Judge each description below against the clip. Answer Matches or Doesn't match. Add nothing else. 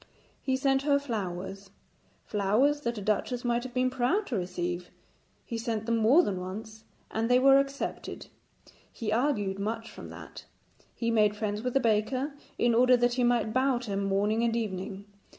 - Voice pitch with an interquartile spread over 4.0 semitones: Doesn't match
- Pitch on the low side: Doesn't match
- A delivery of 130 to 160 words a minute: Doesn't match